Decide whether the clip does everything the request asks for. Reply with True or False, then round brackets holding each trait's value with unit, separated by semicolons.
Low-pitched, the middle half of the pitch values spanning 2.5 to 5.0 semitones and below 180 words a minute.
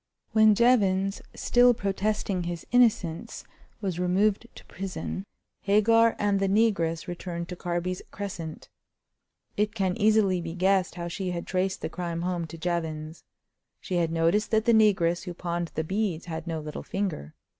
False (185 Hz; 3.3 semitones; 155 wpm)